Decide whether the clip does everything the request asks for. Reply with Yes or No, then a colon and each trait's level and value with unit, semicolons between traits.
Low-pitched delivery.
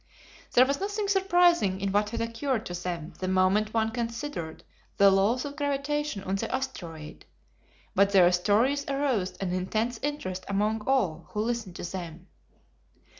No: high, 215 Hz